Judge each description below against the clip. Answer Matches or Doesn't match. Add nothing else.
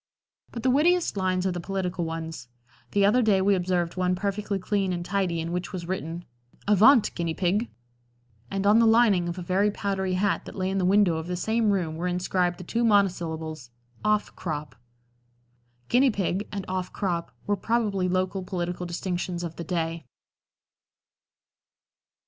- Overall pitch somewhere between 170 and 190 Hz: Matches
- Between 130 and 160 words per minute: Doesn't match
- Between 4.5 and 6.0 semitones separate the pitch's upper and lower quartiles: Doesn't match